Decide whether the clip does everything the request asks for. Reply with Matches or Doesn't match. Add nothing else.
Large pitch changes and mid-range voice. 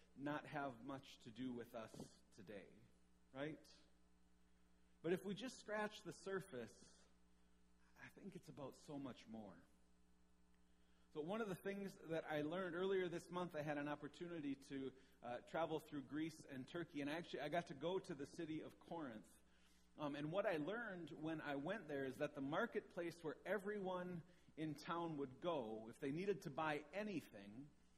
Matches